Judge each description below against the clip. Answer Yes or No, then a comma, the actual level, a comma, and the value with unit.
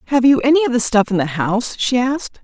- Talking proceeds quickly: Yes, fast, 270 wpm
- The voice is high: Yes, high, 245 Hz